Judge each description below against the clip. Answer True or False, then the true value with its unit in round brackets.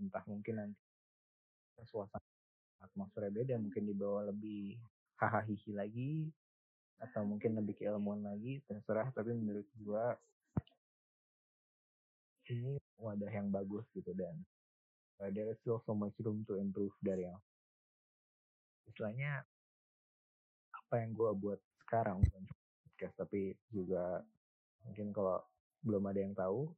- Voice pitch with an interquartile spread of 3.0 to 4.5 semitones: False (2.4 semitones)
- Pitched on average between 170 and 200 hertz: False (105 Hz)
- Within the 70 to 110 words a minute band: False (120 wpm)